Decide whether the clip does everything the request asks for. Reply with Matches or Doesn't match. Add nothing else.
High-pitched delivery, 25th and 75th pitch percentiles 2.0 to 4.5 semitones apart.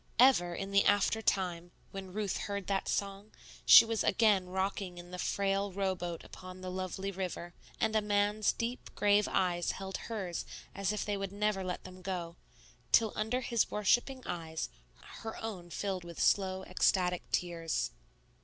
Matches